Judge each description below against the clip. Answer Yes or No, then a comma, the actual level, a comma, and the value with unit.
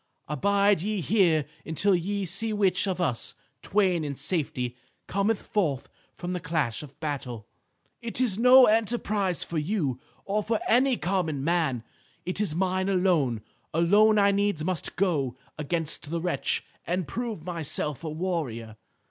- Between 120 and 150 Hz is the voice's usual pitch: No, medium, 180 Hz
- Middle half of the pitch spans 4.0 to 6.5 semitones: Yes, average, 5.0 semitones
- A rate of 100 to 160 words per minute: Yes, average, 150 wpm